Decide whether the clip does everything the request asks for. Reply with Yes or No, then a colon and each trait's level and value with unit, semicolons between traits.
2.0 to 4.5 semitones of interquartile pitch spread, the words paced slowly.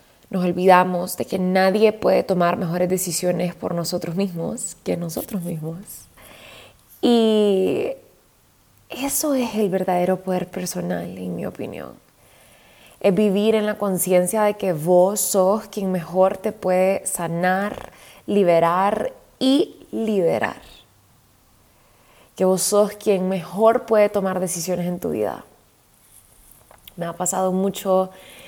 Yes: narrow, 2.5 semitones; slow, 120 wpm